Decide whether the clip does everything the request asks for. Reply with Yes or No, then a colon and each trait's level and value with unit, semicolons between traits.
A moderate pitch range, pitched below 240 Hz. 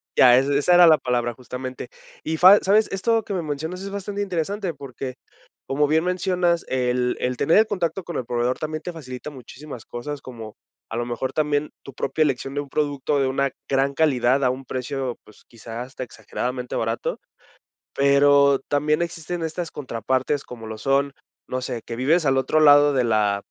Yes: average, 4.1 semitones; medium, 140 Hz